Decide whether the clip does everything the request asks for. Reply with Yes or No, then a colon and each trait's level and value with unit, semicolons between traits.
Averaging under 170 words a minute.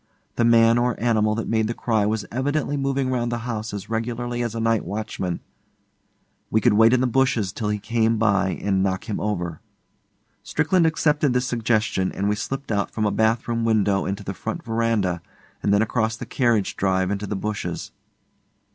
No: average, 190 wpm